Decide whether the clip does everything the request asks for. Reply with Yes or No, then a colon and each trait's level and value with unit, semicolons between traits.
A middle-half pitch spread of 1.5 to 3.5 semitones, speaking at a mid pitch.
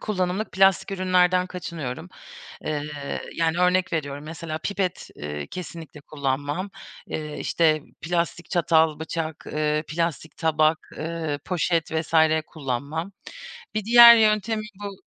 Yes: average, 3.1 semitones; medium, 165 Hz